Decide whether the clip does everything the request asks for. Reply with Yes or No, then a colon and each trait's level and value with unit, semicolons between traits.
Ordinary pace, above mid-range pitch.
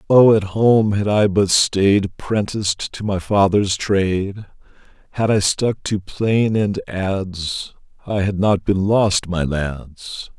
No: average, 150 wpm; low, 100 Hz